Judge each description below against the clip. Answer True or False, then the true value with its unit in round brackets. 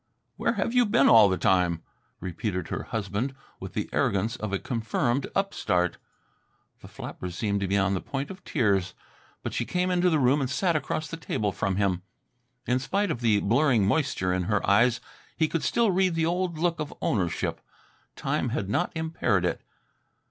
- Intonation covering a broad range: True (8.5 semitones)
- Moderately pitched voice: False (120 Hz)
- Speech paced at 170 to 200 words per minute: True (185 wpm)